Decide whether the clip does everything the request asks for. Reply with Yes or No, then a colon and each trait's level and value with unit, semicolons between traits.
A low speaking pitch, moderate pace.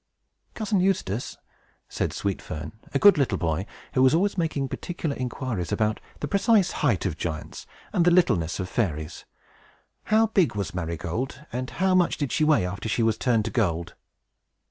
Yes: low, 125 Hz; average, 170 wpm